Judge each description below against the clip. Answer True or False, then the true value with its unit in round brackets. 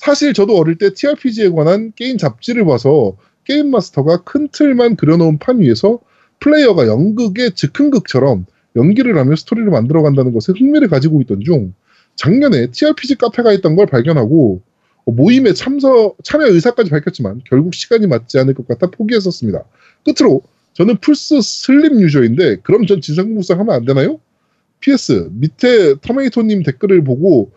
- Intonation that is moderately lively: False (8.8 semitones)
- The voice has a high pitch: True (200 Hz)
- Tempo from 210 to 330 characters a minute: False (365 characters per minute)